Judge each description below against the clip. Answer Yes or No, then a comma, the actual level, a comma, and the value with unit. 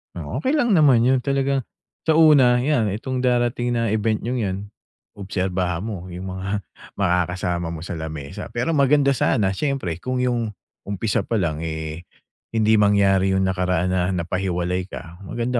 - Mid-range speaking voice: No, low, 100 Hz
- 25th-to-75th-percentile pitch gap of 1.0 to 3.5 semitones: No, wide, 5.7 semitones